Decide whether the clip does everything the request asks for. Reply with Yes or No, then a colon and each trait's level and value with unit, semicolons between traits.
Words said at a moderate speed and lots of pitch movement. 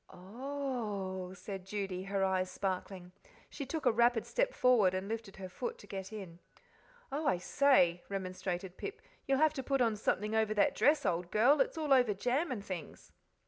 Yes: average, 190 wpm; wide, 6.1 semitones